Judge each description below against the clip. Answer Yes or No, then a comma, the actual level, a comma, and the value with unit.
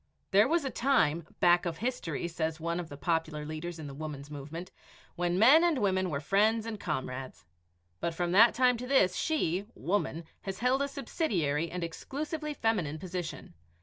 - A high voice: No, medium, 175 Hz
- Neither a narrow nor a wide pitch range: No, wide, 6.4 semitones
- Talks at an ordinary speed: Yes, average, 180 wpm